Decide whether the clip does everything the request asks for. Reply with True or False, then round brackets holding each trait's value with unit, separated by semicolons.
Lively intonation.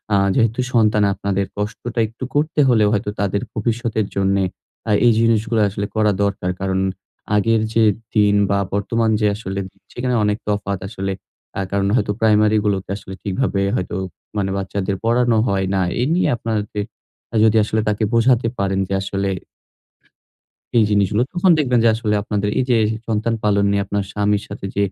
False (2.4 semitones)